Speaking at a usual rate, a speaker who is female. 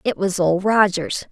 Yes: average, 185 wpm; female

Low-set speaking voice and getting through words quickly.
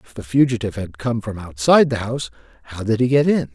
Yes: low, 115 Hz; fast, 235 wpm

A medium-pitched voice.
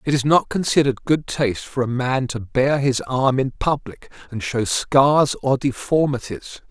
No: low, 130 Hz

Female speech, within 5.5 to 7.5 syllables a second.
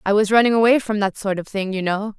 Yes: female; 6.3 syllables/s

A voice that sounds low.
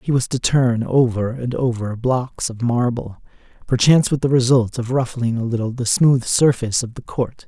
Yes: low, 125 Hz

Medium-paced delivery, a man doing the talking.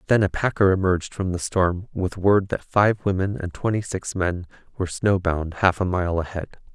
Yes: average, 195 wpm; male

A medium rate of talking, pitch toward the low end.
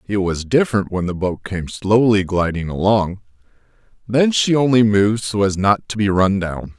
Yes: average, 185 wpm; low, 105 Hz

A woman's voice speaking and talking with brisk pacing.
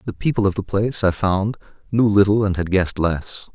No: male; fast, 220 wpm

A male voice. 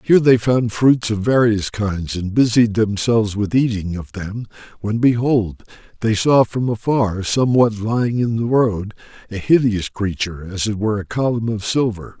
Yes: male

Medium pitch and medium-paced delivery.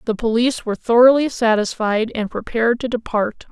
No: high, 230 Hz; average, 155 wpm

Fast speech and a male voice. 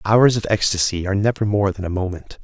Yes: fast, 220 wpm; male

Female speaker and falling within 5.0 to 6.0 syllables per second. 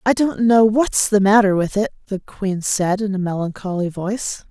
No: female; 4.8 syllables/s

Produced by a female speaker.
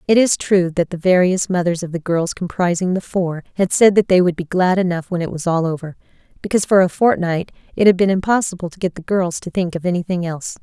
Yes: female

